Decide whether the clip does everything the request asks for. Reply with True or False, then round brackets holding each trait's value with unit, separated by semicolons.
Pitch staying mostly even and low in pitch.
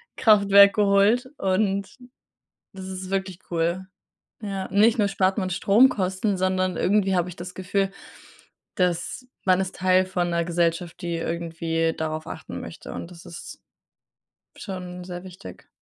False (2.1 semitones; 185 Hz)